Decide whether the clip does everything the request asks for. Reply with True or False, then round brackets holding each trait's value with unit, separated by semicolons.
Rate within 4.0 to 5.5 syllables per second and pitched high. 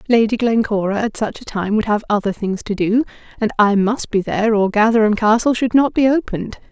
False (5.7 syllables/s; 220 Hz)